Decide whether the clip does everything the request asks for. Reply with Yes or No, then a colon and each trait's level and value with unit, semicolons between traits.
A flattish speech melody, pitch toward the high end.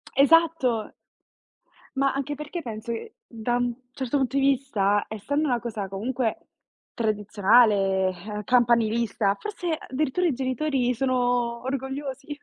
No: average, 3.9 semitones; high, 245 Hz